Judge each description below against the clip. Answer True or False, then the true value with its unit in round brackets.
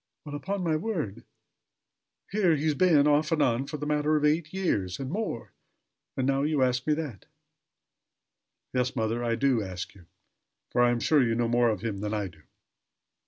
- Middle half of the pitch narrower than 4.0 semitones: False (4.9 semitones)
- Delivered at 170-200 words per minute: True (190 wpm)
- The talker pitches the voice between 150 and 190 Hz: False (135 Hz)